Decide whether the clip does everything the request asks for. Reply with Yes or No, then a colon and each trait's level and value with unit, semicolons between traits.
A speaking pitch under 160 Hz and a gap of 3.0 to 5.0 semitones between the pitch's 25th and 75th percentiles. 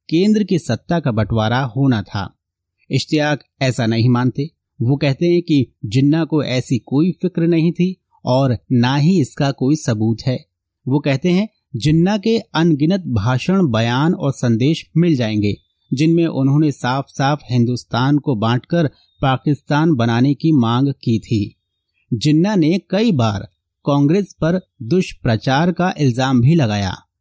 No: low, 135 Hz; wide, 5.5 semitones